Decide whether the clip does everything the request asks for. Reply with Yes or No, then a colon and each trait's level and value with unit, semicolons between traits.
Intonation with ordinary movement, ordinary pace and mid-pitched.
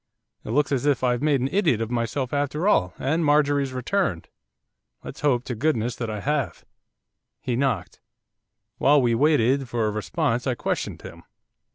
No: average, 3.7 semitones; average, 170 wpm; low, 130 Hz